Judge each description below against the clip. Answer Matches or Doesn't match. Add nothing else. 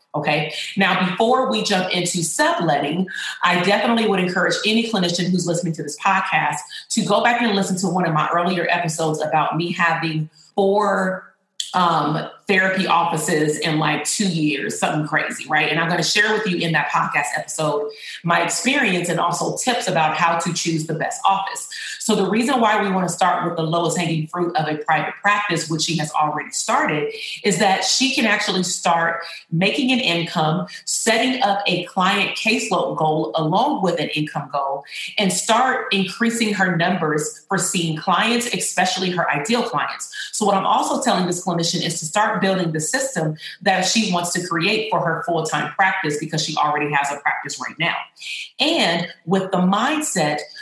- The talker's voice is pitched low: Doesn't match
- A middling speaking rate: Matches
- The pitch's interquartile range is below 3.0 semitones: Doesn't match